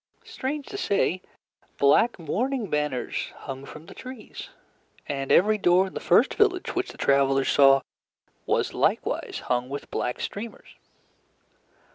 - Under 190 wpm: Yes, slow, 135 wpm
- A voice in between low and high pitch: Yes, medium, 175 Hz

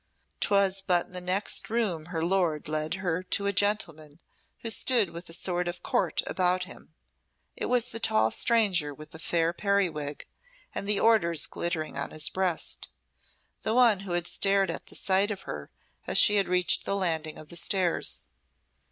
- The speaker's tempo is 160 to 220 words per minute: Yes, average, 180 wpm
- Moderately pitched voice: Yes, medium, 180 Hz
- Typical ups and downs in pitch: Yes, average, 3.7 semitones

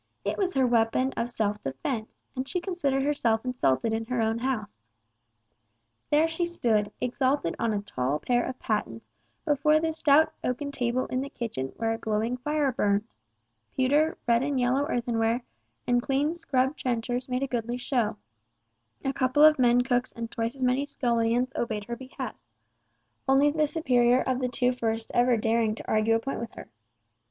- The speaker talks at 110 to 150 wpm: No, average, 175 wpm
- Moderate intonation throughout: Yes, average, 3.1 semitones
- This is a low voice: No, high, 245 Hz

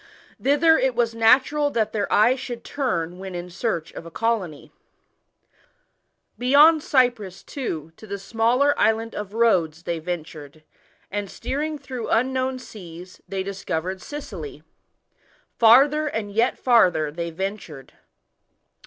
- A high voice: Yes, high, 220 Hz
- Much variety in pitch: Yes, wide, 6.4 semitones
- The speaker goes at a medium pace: No, slow, 130 wpm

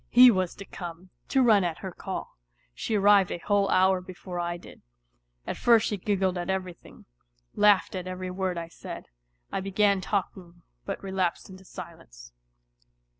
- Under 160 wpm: No, average, 165 wpm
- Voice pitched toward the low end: No, medium, 185 Hz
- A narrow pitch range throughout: Yes, narrow, 2.0 semitones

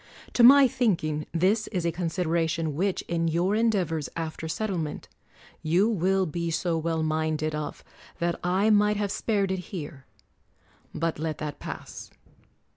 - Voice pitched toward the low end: No, medium, 170 Hz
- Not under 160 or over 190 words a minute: No, average, 145 wpm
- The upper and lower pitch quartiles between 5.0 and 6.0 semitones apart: No, average, 3.8 semitones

